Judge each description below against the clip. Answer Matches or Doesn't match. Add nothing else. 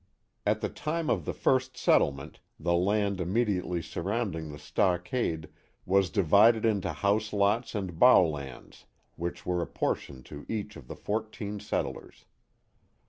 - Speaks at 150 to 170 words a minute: Doesn't match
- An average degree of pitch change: Matches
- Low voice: Matches